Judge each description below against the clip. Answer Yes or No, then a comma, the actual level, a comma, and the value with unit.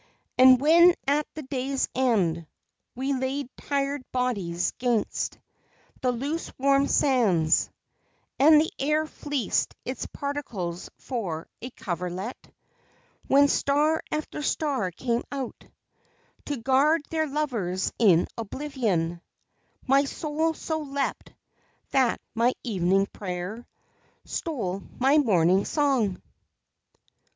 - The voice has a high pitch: Yes, very high, 260 Hz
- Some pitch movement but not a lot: No, wide, 6.4 semitones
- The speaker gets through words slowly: Yes, slow, 105 wpm